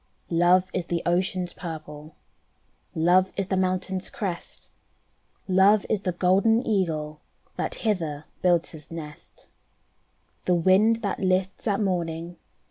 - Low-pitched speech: No, medium, 185 Hz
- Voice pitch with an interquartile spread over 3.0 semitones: No, narrow, 2.4 semitones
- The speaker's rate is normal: No, slow, 125 wpm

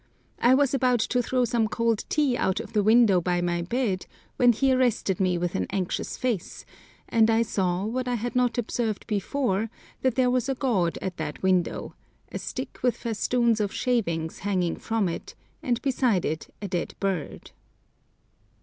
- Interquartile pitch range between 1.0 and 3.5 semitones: No, average, 4.8 semitones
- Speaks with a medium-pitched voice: No, high, 225 Hz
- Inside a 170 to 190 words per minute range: Yes, average, 175 wpm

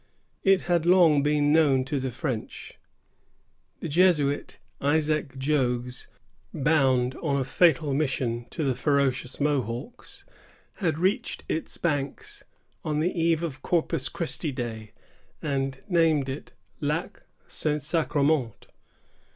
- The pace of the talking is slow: Yes, slow, 120 wpm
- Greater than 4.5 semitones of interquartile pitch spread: No, average, 3.4 semitones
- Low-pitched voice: No, medium, 145 Hz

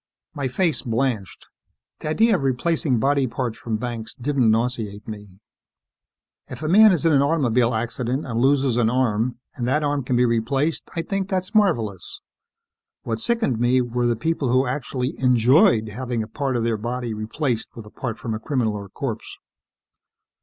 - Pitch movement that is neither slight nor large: Yes, average, 3.9 semitones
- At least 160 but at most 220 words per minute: Yes, average, 175 wpm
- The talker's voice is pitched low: Yes, low, 125 Hz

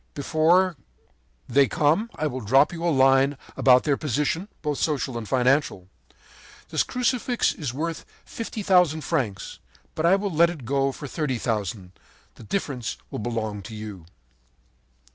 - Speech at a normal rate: Yes, average, 150 wpm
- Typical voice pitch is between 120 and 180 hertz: Yes, medium, 140 Hz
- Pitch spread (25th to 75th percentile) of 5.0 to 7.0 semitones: Yes, wide, 5.5 semitones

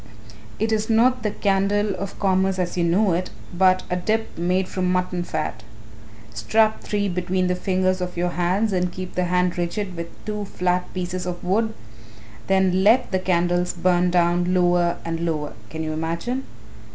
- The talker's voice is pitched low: No, medium, 180 Hz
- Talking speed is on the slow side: No, average, 175 wpm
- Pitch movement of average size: No, narrow, 1.9 semitones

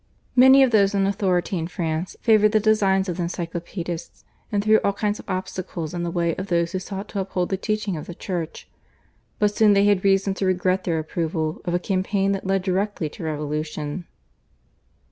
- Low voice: No, medium, 185 Hz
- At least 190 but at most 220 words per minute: Yes, average, 200 wpm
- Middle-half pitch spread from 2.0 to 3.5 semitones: Yes, average, 2.8 semitones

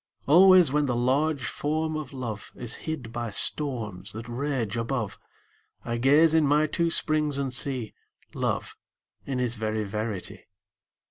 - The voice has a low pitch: Yes, low, 130 Hz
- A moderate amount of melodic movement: Yes, average, 4.7 semitones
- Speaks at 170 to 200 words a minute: No, average, 145 wpm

